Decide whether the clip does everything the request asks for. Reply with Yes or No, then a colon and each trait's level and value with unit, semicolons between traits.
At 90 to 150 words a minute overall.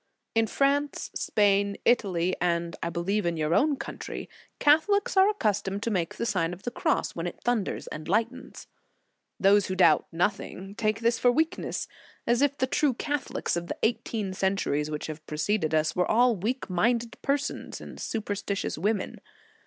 No: average, 175 wpm